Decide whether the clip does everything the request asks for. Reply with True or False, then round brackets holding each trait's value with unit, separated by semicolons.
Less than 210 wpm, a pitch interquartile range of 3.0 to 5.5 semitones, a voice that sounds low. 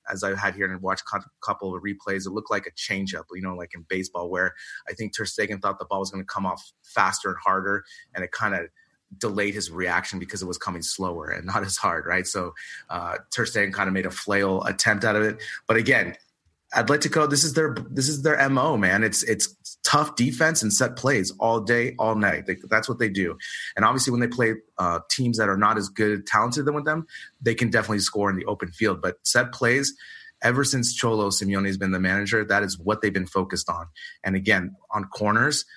False (240 wpm; 4.7 semitones; 110 Hz)